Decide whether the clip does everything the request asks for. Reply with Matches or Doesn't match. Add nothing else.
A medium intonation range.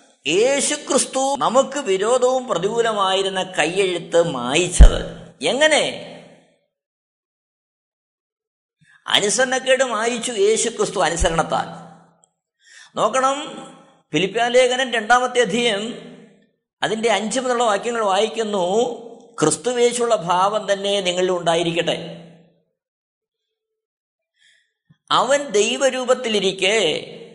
Matches